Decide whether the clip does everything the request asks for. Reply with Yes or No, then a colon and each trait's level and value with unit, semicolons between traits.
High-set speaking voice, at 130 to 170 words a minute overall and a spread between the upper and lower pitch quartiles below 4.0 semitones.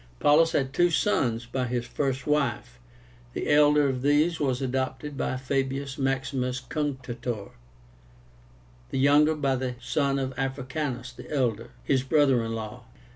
No: low, 135 Hz; average, 140 wpm; narrow, 2.5 semitones